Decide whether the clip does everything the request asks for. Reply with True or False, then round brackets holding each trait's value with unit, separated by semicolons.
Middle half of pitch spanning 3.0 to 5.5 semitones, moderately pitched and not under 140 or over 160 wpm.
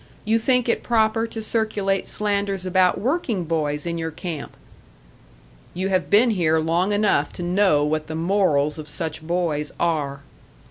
True (4.7 semitones; 180 Hz; 155 wpm)